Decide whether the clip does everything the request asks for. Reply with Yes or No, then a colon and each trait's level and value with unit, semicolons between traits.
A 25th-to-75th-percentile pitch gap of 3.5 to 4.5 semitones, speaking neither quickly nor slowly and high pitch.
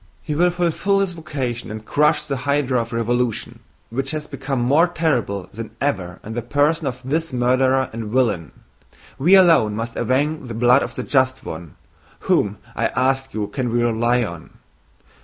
No: average, 4.2 semitones; average, 175 wpm; low, 130 Hz